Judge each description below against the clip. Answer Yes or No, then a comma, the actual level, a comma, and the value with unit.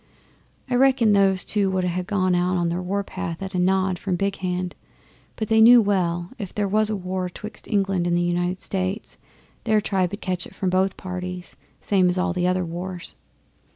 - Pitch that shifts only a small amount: Yes, narrow, 1.9 semitones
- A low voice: No, medium, 185 Hz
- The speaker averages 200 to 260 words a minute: Yes, fast, 205 wpm